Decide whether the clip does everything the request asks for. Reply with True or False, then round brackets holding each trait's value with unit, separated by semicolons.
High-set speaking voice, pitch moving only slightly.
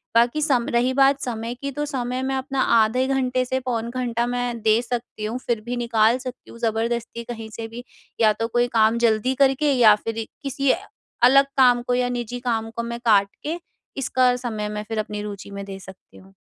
True (240 Hz; 2.3 semitones)